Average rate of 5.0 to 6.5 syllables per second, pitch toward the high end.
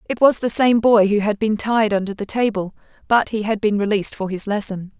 Yes: 5.5 syllables/s; high, 210 Hz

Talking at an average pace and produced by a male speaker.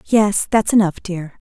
No: average, 165 wpm; female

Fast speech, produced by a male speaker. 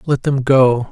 No: average, 195 wpm; male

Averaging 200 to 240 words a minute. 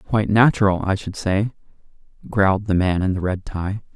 No: average, 180 wpm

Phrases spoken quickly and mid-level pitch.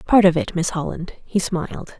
Yes: fast, 210 wpm; medium, 180 Hz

